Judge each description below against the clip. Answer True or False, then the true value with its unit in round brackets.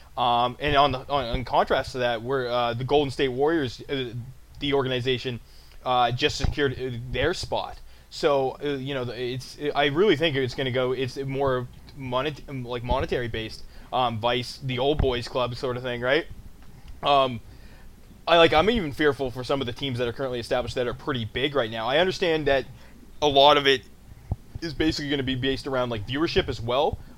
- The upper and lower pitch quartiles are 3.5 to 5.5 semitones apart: False (2.5 semitones)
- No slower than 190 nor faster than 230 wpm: True (200 wpm)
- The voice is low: True (130 Hz)